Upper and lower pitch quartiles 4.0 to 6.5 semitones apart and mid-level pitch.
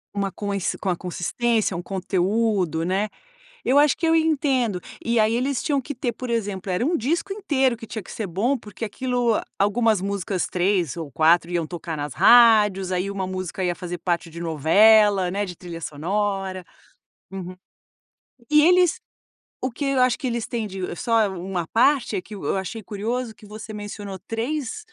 No: average, 4.6 semitones; high, 205 Hz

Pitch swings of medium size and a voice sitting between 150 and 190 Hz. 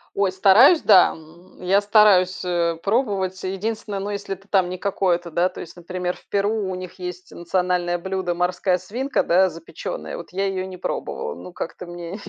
No: narrow, 1.9 semitones; medium, 185 Hz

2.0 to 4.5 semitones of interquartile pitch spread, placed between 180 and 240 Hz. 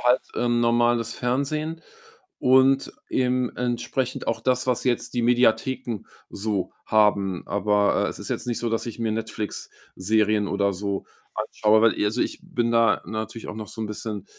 No: narrow, 2.5 semitones; low, 115 Hz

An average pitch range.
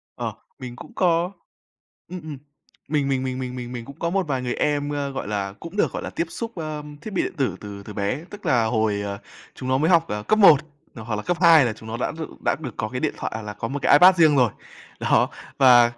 No: wide, 6.2 semitones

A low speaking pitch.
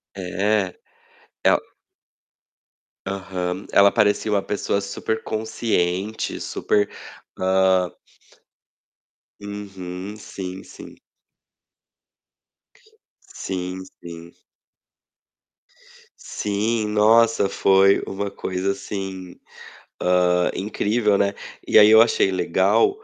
Yes: low, 100 Hz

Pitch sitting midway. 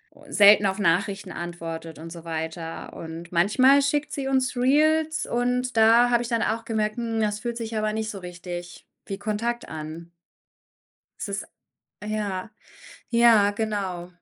No: high, 215 Hz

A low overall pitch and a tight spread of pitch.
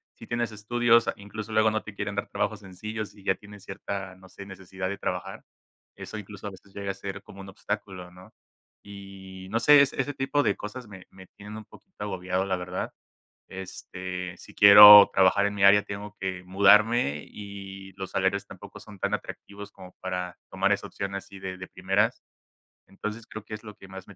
Yes: low, 100 Hz; narrow, 1.8 semitones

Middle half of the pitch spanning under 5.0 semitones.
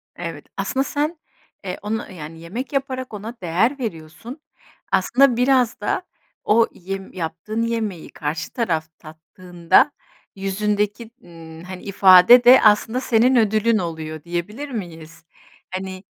No: wide, 5.5 semitones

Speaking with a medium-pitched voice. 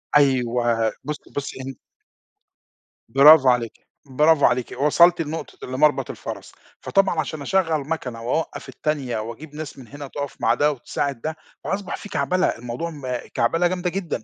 Yes: medium, 145 Hz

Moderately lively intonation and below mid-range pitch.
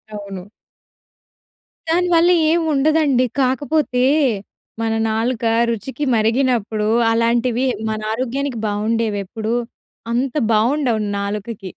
No: average, 3.8 semitones; high, 235 Hz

